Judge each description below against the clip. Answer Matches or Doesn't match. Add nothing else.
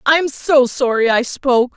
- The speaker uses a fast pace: Doesn't match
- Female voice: Matches